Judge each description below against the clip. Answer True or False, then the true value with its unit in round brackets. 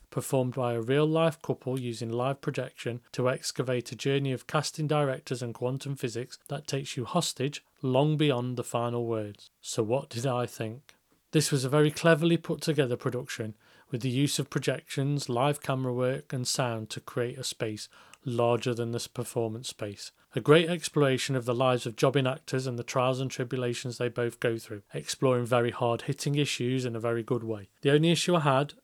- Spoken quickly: False (195 wpm)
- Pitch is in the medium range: False (130 Hz)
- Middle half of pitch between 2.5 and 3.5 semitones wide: True (3.0 semitones)